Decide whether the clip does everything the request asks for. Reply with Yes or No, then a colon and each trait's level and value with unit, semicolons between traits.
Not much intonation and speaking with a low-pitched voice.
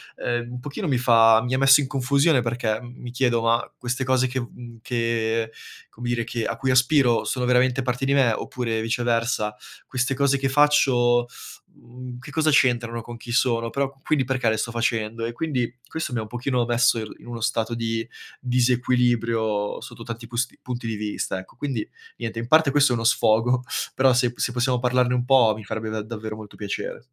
Yes: narrow, 2.0 semitones; low, 120 Hz